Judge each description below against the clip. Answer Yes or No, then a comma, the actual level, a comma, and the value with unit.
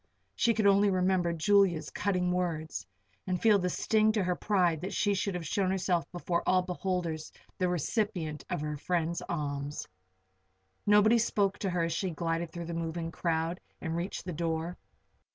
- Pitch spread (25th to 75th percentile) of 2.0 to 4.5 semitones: Yes, average, 2.8 semitones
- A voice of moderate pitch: Yes, medium, 180 Hz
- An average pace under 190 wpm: Yes, average, 170 wpm